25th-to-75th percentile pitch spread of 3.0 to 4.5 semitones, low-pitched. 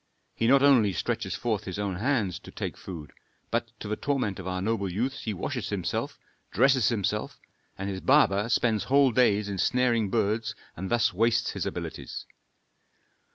Yes: average, 3.9 semitones; low, 110 Hz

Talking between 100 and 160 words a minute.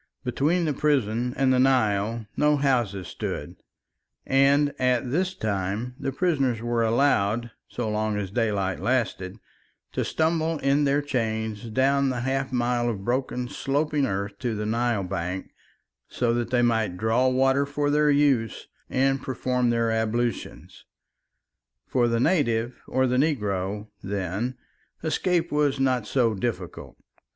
Yes: average, 140 wpm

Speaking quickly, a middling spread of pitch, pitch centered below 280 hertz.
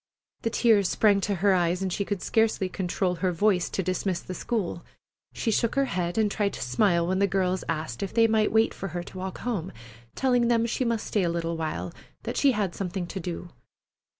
Yes: fast, 220 wpm; average, 3.8 semitones; high, 190 Hz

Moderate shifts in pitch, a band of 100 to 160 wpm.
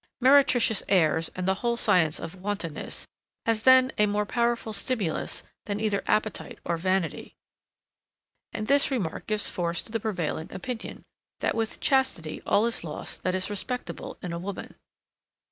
Yes: average, 4.6 semitones; average, 150 wpm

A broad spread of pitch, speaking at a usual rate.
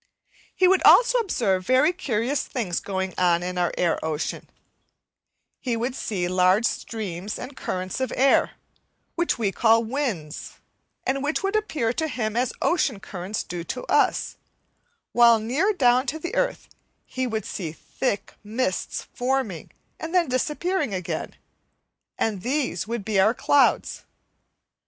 Yes: wide, 6.6 semitones; average, 145 wpm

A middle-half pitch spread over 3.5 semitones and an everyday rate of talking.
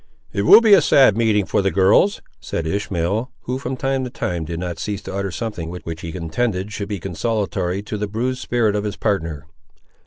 No: average, 4.5 semitones; fast, 210 wpm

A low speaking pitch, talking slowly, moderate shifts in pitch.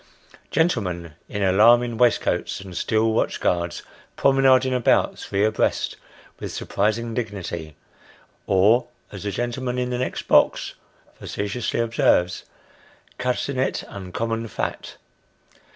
Yes: low, 115 Hz; slow, 115 wpm; average, 4.0 semitones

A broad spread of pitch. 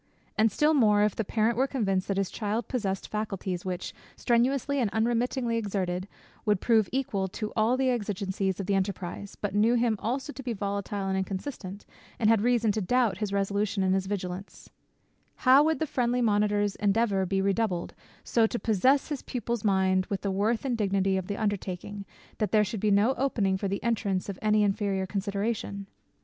No: average, 3.2 semitones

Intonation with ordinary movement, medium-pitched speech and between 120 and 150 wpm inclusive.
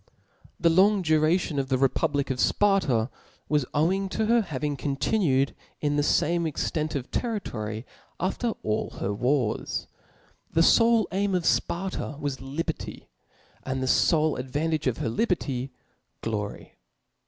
No: wide, 5.8 semitones; medium, 150 Hz; slow, 135 wpm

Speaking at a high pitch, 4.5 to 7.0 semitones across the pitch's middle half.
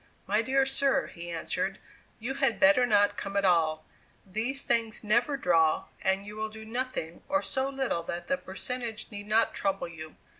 Yes: high, 215 Hz; average, 5.1 semitones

